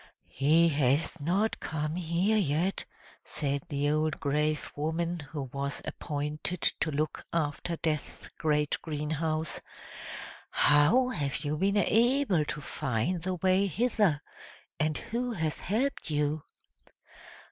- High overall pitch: No, medium, 155 Hz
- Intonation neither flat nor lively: Yes, average, 3.7 semitones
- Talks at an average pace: No, slow, 120 wpm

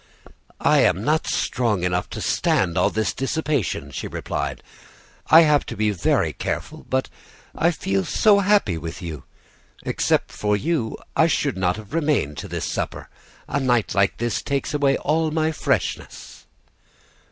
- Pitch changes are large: Yes, wide, 8.1 semitones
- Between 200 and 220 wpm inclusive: No, average, 155 wpm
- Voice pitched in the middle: No, low, 125 Hz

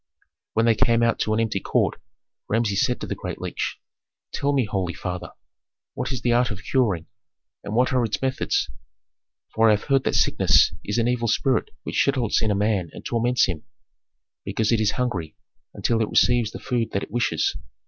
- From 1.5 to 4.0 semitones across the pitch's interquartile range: Yes, average, 3.0 semitones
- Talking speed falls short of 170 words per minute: No, average, 200 wpm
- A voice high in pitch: No, low, 115 Hz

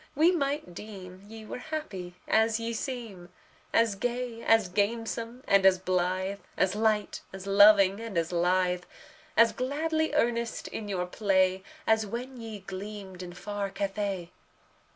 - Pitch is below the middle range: No, high, 205 Hz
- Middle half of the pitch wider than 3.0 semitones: Yes, average, 3.6 semitones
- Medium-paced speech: Yes, average, 145 wpm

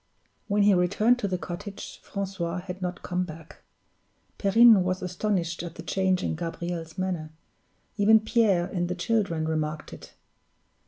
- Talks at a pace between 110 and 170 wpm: Yes, average, 150 wpm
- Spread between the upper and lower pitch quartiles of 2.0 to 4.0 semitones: Yes, average, 2.7 semitones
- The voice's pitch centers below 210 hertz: Yes, medium, 185 Hz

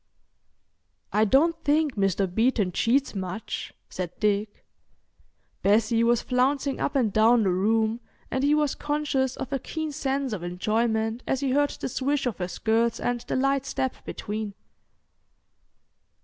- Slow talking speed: No, average, 150 wpm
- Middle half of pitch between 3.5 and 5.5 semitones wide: Yes, average, 4.3 semitones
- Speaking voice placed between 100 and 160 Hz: No, high, 235 Hz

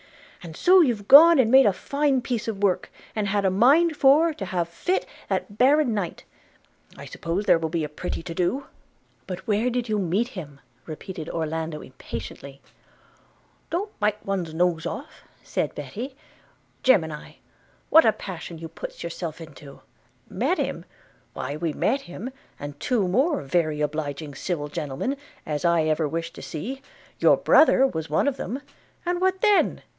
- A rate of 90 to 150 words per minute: No, average, 170 wpm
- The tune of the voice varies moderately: No, wide, 8.3 semitones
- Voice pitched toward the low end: No, medium, 185 Hz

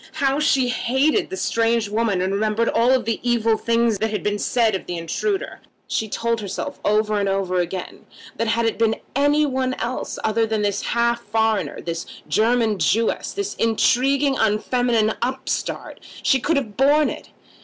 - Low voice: No, high, 230 Hz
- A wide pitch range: No, average, 3.2 semitones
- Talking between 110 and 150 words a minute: No, average, 165 wpm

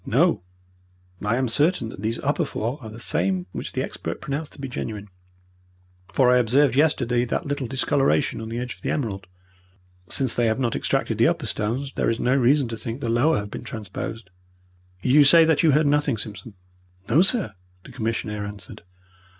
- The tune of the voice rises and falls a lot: No, average, 4.3 semitones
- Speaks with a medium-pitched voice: No, low, 120 Hz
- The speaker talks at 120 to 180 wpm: No, average, 190 wpm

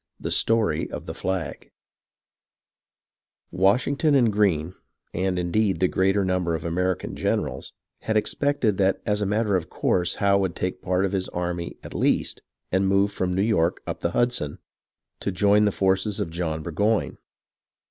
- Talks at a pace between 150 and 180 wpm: Yes, average, 170 wpm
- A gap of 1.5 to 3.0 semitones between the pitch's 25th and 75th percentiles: Yes, average, 2.7 semitones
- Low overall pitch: Yes, very low, 95 Hz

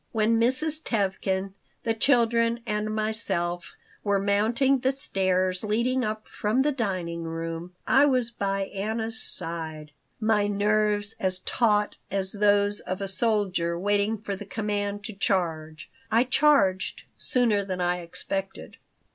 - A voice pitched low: No, high, 205 Hz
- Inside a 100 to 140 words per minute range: Yes, slow, 135 wpm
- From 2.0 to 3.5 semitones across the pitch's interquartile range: Yes, average, 3.2 semitones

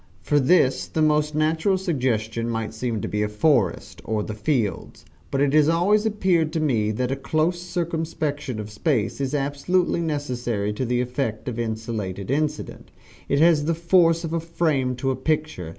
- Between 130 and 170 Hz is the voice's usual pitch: Yes, medium, 140 Hz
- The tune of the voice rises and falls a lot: Yes, wide, 5.7 semitones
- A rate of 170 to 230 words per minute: Yes, average, 180 wpm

